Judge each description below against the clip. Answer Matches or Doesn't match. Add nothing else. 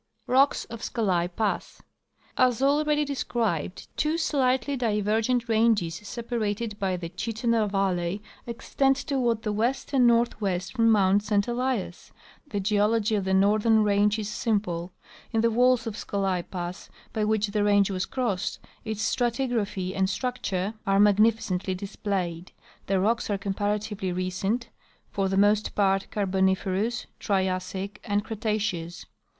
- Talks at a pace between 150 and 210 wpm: Doesn't match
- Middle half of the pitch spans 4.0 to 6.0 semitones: Doesn't match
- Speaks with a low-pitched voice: Doesn't match